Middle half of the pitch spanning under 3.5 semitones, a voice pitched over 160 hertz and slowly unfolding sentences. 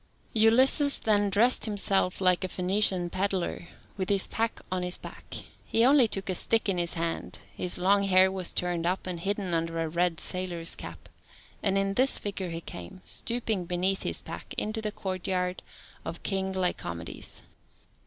No: narrow, 2.4 semitones; high, 190 Hz; average, 170 wpm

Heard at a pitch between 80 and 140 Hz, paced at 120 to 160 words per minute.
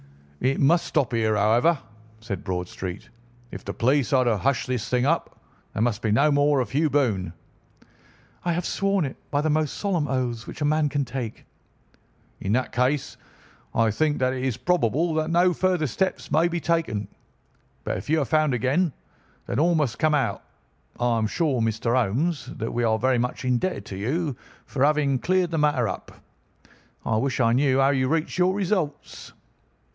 No: low, 135 Hz; average, 185 wpm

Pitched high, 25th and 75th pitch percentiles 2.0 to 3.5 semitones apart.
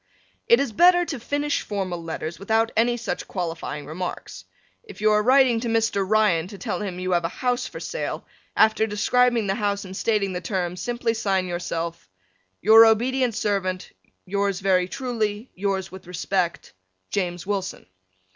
No: high, 205 Hz; average, 3.9 semitones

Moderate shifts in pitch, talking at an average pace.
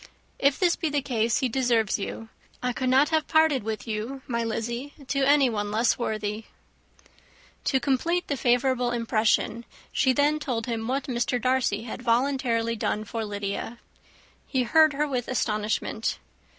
Yes: average, 3.4 semitones; average, 155 wpm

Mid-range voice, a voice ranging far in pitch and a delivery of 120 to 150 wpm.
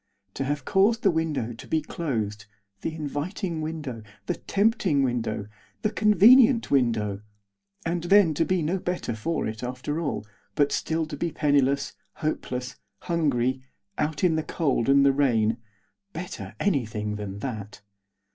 Yes: medium, 145 Hz; wide, 5.7 semitones; average, 145 wpm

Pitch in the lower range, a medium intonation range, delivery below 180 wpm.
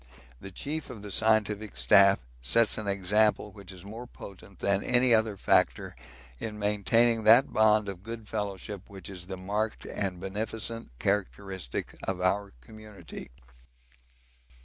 No: low, 105 Hz; narrow, 2.1 semitones; average, 140 wpm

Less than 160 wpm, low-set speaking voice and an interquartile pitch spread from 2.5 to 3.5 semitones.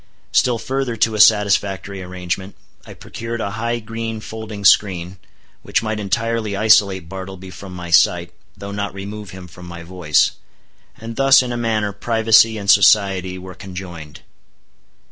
Yes: average, 150 wpm; low, 100 Hz; average, 3.2 semitones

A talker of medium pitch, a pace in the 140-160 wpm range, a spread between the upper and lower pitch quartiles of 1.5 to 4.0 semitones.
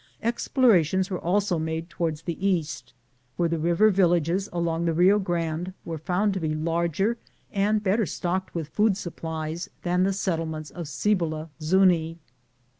Yes: medium, 175 Hz; average, 150 wpm; average, 2.9 semitones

